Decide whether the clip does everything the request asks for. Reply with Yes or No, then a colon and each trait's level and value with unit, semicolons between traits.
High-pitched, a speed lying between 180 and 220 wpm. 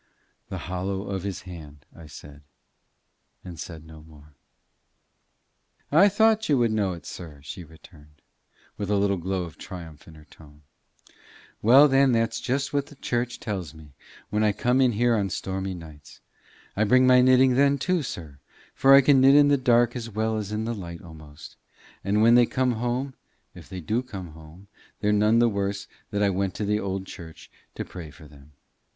No: low, 100 Hz; average, 195 wpm